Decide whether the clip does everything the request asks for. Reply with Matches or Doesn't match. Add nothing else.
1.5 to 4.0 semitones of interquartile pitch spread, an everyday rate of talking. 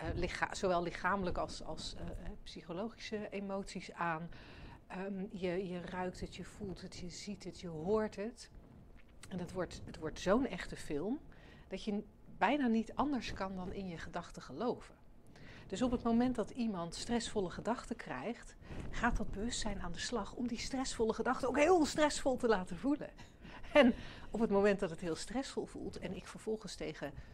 Doesn't match